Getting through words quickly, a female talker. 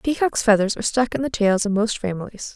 Yes: fast, 235 wpm; female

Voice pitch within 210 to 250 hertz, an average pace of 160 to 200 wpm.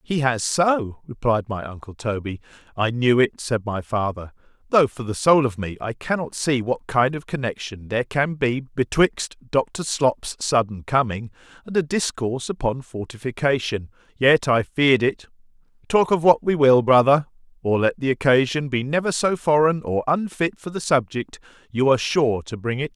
No: low, 130 Hz; average, 165 wpm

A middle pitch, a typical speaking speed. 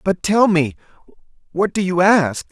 Yes: medium, 180 Hz; average, 165 wpm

